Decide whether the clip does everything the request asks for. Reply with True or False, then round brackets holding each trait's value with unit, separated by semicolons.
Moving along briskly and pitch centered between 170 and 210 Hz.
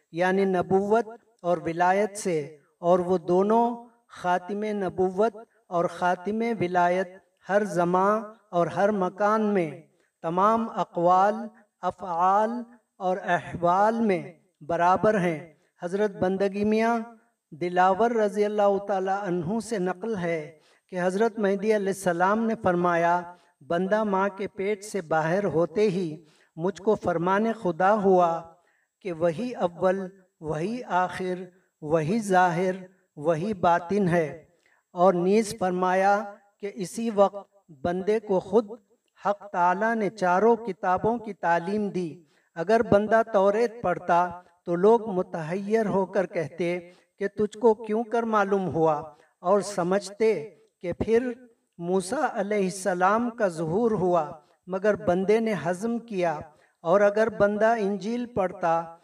False (125 wpm; 190 Hz)